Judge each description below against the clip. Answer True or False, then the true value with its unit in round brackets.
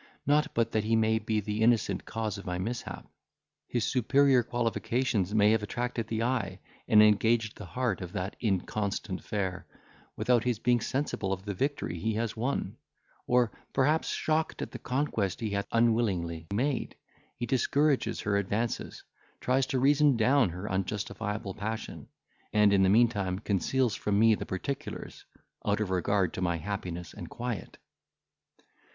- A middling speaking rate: True (160 wpm)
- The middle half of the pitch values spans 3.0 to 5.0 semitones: True (3.6 semitones)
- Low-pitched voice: True (110 Hz)